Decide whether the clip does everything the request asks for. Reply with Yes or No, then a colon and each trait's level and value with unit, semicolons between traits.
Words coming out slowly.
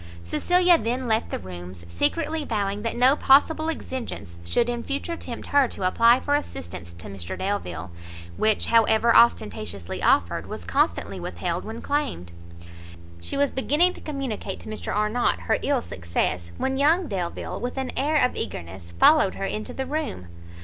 No: average, 165 wpm